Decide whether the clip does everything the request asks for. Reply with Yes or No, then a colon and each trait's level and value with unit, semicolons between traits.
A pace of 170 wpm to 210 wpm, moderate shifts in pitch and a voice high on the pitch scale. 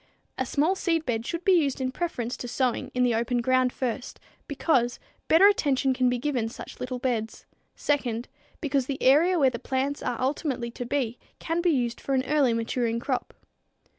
Yes: average, 185 wpm; average, 3.1 semitones; very high, 260 Hz